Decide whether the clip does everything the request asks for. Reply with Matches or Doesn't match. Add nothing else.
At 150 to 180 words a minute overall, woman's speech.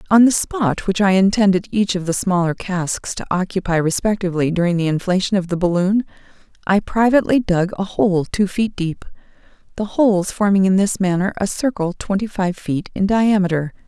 Matches